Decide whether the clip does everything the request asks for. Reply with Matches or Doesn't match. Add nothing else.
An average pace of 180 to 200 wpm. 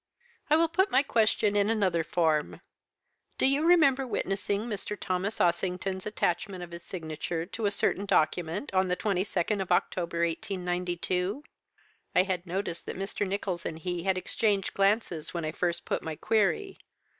Doesn't match